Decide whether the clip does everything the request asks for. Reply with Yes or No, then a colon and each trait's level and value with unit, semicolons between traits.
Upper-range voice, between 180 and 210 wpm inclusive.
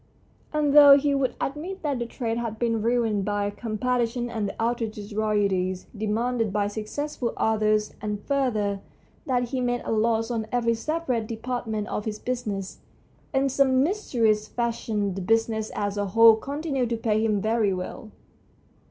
No: high, 225 Hz; average, 160 wpm